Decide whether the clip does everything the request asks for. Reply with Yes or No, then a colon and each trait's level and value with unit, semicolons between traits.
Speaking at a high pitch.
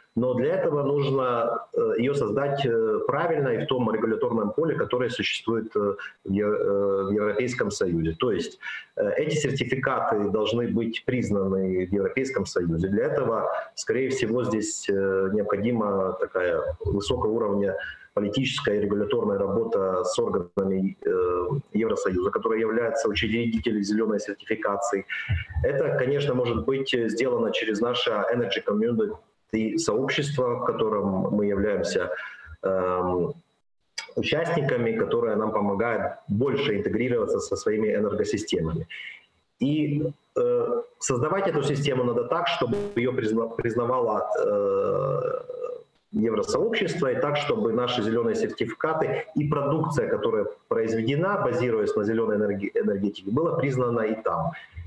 No: low, 125 Hz